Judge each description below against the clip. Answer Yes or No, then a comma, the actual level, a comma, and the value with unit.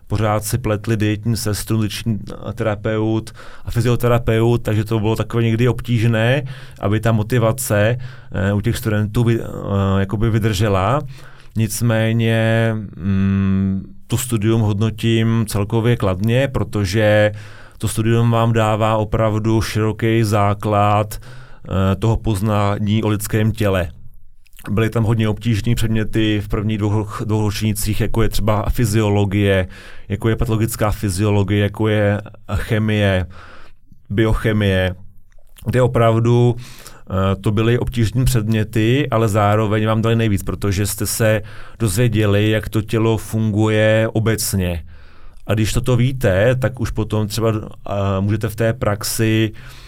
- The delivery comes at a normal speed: Yes, average, 125 wpm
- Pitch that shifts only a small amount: Yes, narrow, 1.7 semitones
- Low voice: Yes, low, 110 Hz